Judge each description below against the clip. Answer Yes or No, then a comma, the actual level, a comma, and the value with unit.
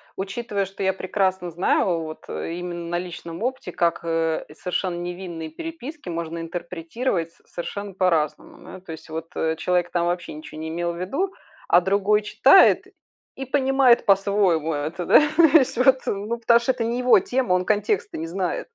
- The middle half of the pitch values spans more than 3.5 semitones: Yes, average, 4.2 semitones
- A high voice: No, medium, 180 Hz